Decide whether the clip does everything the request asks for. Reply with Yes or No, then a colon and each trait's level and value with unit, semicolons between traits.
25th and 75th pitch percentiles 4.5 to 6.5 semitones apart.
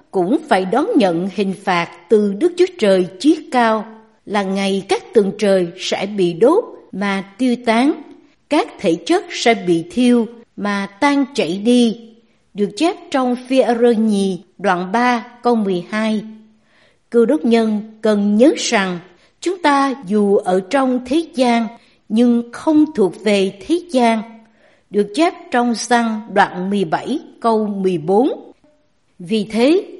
Yes: average, 5.0 semitones